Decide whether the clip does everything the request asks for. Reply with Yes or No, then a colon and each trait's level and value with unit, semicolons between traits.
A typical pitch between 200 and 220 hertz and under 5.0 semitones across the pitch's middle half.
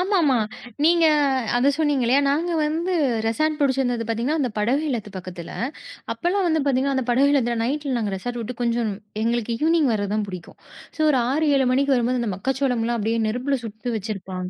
No: very high, 250 Hz; average, 4.0 semitones